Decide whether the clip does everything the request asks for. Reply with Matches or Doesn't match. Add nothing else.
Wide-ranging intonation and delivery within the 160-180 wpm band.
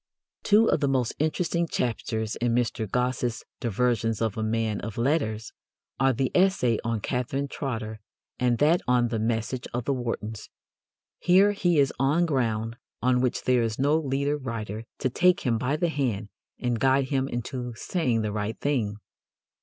Doesn't match